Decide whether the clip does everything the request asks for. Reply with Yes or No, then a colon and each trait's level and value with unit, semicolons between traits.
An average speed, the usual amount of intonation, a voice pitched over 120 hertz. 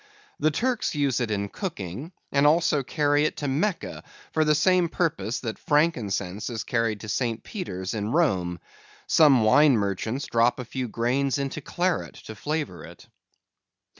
No: average, 160 wpm; wide, 5.8 semitones; low, 135 Hz